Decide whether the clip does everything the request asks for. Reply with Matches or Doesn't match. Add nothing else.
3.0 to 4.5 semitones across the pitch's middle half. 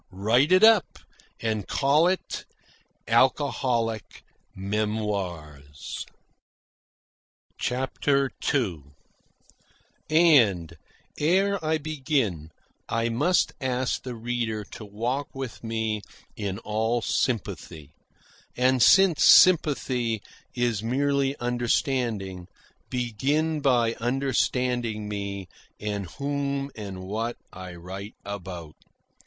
Doesn't match